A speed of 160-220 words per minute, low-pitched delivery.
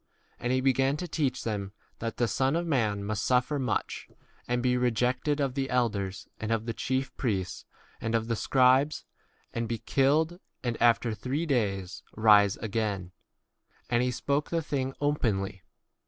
Yes: average, 170 wpm; low, 125 Hz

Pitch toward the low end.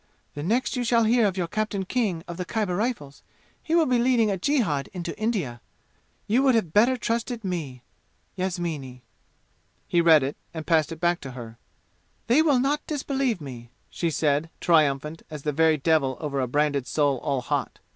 No: medium, 175 Hz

